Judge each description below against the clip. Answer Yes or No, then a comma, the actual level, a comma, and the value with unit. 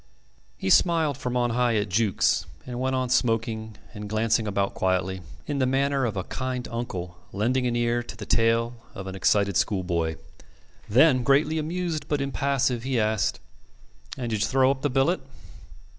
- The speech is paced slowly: No, average, 175 wpm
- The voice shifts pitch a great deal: No, average, 4.0 semitones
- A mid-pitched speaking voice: No, low, 120 Hz